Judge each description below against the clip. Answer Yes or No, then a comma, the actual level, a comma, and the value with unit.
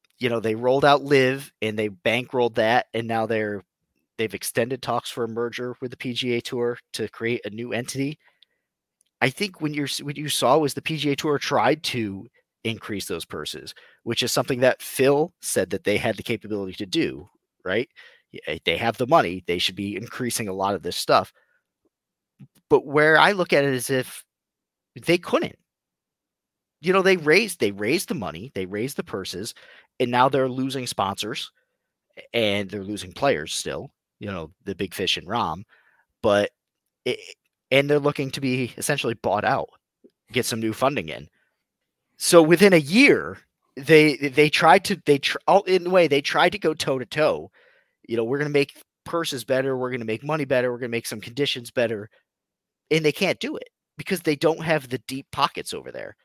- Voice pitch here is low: Yes, low, 130 Hz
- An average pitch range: Yes, average, 4.7 semitones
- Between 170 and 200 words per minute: Yes, average, 190 wpm